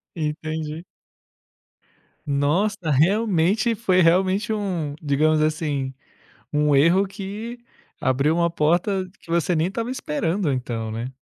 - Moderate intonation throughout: Yes, average, 4.4 semitones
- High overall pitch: No, medium, 165 Hz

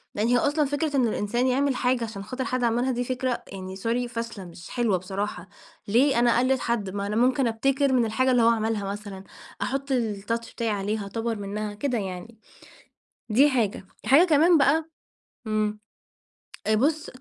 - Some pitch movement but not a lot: Yes, average, 3.7 semitones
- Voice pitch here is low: No, high, 235 Hz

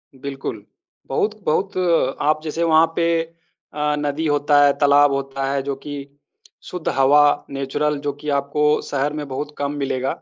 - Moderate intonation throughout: No, narrow, 1.5 semitones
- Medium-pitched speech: Yes, medium, 145 Hz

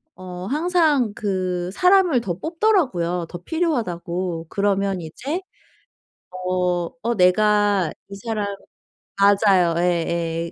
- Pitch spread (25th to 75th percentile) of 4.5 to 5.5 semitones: Yes, average, 5.2 semitones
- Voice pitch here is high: Yes, high, 195 Hz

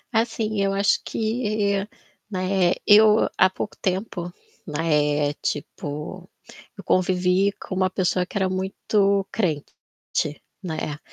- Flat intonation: Yes, narrow, 2.3 semitones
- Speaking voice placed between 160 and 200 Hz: Yes, high, 190 Hz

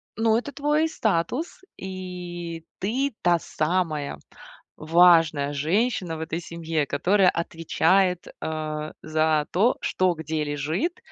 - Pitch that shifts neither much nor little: Yes, average, 3.6 semitones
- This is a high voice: No, medium, 170 Hz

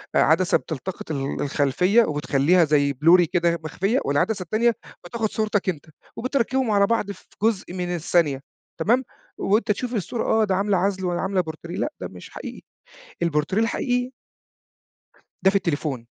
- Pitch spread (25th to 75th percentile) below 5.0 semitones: No, average, 5.3 semitones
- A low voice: No, medium, 185 Hz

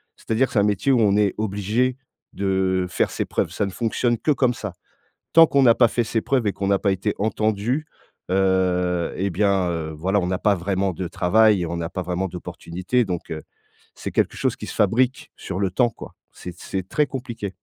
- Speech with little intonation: No, average, 3.7 semitones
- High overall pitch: No, low, 100 Hz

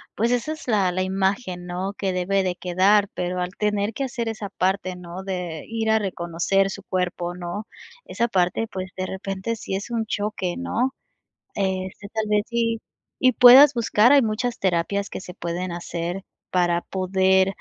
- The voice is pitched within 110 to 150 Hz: No, high, 195 Hz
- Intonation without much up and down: No, average, 3.4 semitones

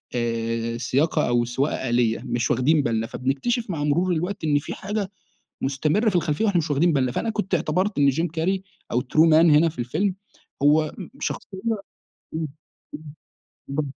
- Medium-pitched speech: Yes, medium, 150 Hz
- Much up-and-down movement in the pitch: Yes, wide, 5.7 semitones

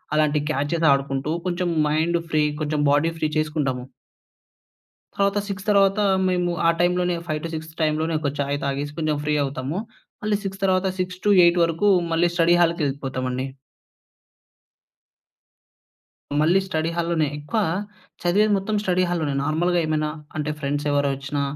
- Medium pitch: Yes, medium, 160 Hz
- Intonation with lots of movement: No, average, 3.4 semitones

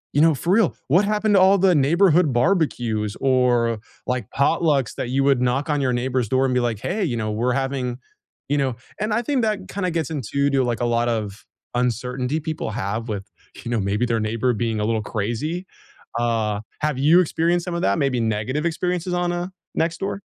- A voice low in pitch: Yes, low, 130 Hz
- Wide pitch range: Yes, wide, 6.2 semitones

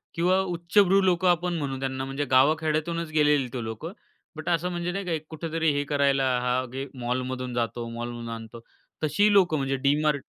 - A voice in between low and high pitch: Yes, medium, 150 Hz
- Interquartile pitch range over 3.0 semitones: Yes, average, 4.7 semitones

